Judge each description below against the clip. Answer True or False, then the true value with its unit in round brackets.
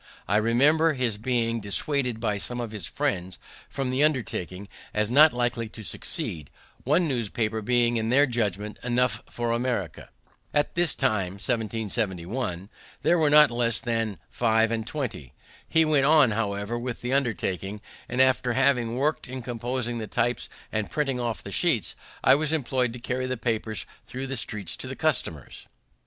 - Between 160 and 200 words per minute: True (165 wpm)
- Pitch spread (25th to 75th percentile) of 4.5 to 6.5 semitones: False (3.4 semitones)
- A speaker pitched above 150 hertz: False (120 Hz)